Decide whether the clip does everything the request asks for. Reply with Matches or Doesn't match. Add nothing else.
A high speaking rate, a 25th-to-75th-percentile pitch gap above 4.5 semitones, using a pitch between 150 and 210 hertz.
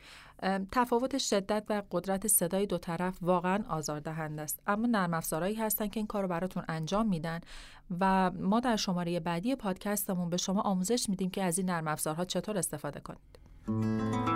Doesn't match